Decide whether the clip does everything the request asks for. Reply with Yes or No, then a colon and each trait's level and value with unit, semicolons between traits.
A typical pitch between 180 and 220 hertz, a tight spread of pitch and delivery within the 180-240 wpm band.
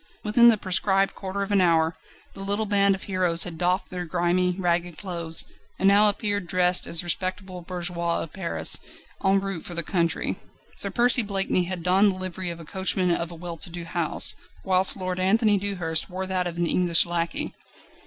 Yes: medium, 185 Hz; narrow, 2.2 semitones; average, 195 wpm